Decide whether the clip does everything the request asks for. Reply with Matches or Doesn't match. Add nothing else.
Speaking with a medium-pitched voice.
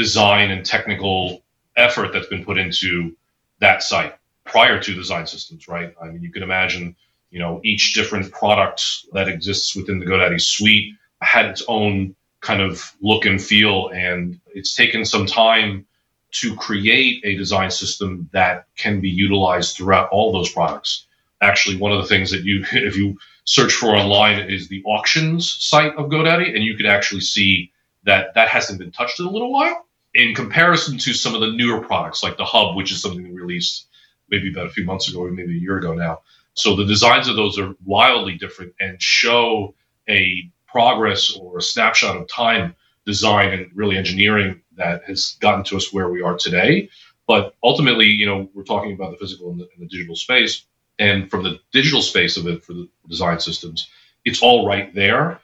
Doesn't match